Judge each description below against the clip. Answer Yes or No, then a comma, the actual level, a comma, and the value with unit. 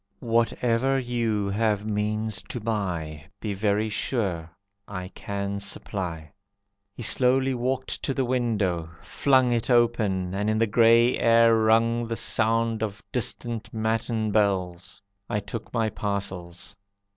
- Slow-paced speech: Yes, slow, 130 wpm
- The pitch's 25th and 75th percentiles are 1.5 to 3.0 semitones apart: Yes, average, 2.7 semitones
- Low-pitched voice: Yes, low, 110 Hz